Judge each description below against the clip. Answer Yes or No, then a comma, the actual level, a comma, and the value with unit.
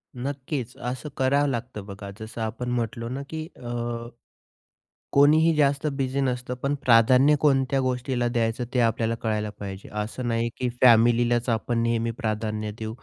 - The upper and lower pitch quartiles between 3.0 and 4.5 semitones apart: No, narrow, 2.5 semitones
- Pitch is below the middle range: Yes, low, 120 Hz